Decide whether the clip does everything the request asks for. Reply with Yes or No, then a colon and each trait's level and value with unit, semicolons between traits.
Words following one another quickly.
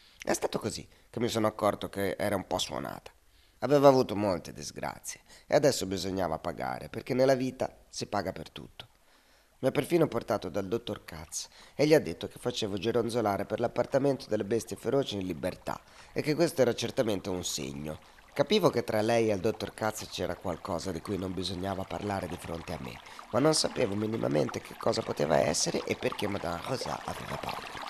Yes: fast, 190 wpm